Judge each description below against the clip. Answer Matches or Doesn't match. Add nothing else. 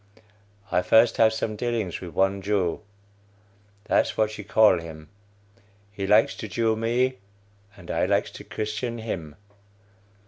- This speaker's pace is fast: Doesn't match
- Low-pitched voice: Matches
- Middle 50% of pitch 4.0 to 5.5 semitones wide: Doesn't match